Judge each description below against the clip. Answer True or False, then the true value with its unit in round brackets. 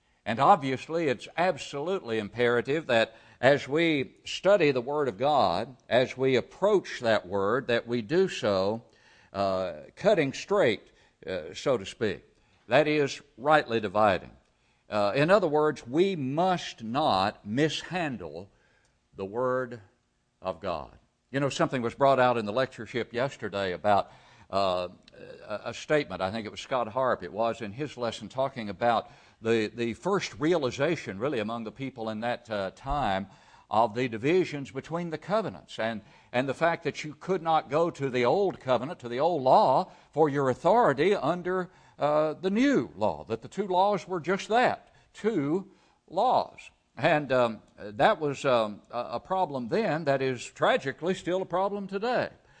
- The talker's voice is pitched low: True (130 Hz)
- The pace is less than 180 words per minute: True (160 wpm)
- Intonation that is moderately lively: False (5.8 semitones)